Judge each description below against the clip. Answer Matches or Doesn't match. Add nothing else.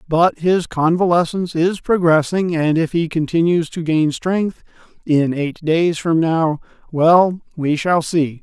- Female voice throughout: Doesn't match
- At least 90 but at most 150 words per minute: Matches